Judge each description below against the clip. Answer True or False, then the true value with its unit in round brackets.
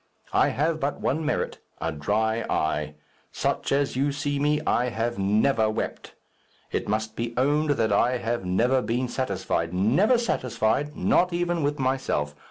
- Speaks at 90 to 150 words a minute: False (160 wpm)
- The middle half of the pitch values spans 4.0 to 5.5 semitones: True (5.0 semitones)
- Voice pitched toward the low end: True (125 Hz)